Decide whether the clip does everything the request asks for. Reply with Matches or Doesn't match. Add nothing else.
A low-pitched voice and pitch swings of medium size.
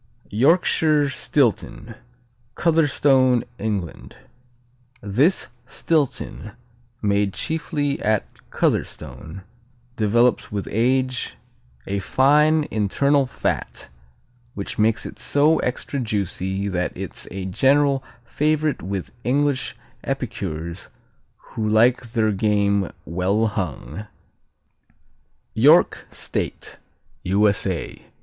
Doesn't match